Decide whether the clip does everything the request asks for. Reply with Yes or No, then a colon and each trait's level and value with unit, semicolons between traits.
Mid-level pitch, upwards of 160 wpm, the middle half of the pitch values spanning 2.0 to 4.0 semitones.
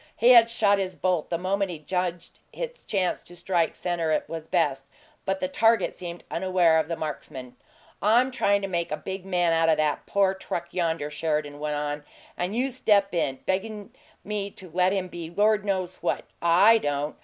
Yes: medium, 180 Hz; average, 190 wpm; average, 3.6 semitones